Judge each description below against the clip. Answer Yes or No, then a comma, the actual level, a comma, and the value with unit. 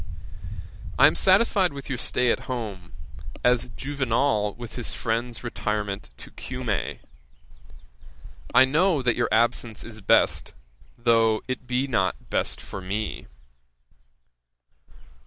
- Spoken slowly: Yes, slow, 120 wpm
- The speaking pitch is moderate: No, low, 120 Hz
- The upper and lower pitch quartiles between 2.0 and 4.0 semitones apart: Yes, average, 3.3 semitones